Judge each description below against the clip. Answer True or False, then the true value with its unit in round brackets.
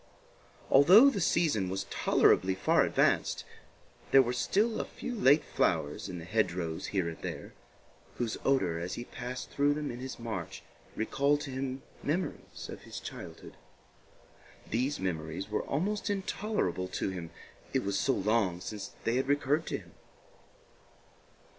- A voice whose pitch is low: True (125 Hz)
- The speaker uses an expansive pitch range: True (7.5 semitones)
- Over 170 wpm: False (155 wpm)